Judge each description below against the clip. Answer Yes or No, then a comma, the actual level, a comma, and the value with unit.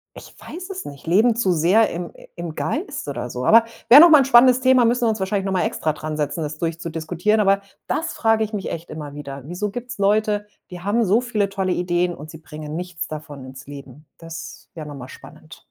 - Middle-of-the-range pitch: Yes, medium, 180 Hz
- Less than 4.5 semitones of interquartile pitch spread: No, wide, 6.2 semitones